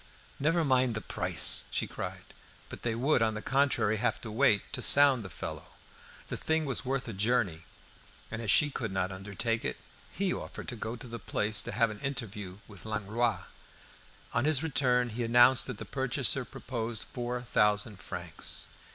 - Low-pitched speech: Yes, low, 120 Hz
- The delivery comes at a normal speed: Yes, average, 180 wpm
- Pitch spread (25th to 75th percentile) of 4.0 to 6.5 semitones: No, average, 3.6 semitones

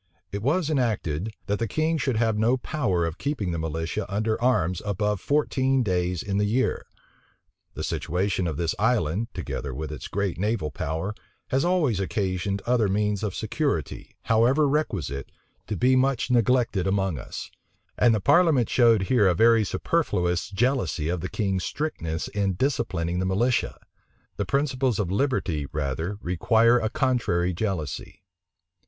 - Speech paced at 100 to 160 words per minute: Yes, average, 155 wpm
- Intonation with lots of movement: Yes, wide, 5.9 semitones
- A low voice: Yes, low, 105 Hz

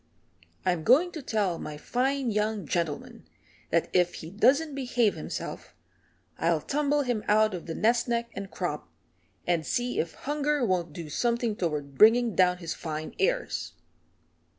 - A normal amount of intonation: No, wide, 6.3 semitones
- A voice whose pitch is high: Yes, high, 215 Hz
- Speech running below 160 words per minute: Yes, average, 150 wpm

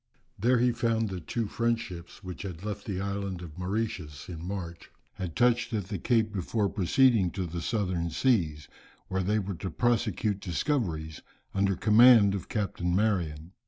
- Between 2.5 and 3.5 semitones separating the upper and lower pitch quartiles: No, average, 4.2 semitones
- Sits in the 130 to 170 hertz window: No, low, 100 Hz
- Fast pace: No, average, 165 wpm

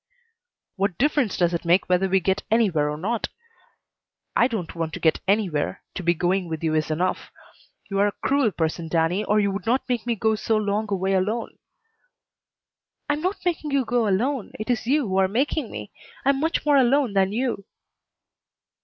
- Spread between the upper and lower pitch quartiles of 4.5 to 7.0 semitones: Yes, average, 5.0 semitones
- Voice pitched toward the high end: Yes, high, 205 Hz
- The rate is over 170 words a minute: Yes, average, 200 wpm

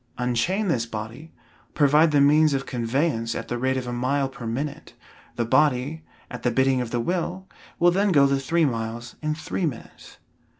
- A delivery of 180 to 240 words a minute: Yes, average, 185 wpm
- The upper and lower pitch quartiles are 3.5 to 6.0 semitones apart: Yes, average, 4.3 semitones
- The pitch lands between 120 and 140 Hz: Yes, low, 135 Hz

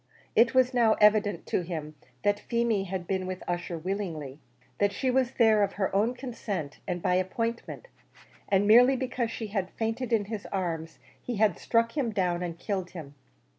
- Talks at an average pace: Yes, average, 180 wpm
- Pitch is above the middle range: Yes, high, 205 Hz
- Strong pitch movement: No, average, 4.3 semitones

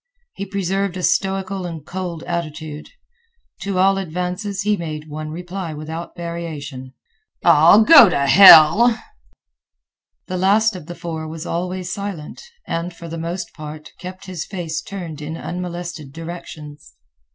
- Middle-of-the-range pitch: Yes, medium, 170 Hz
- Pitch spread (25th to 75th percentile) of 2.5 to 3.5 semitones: Yes, average, 3.1 semitones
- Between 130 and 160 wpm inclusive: Yes, average, 140 wpm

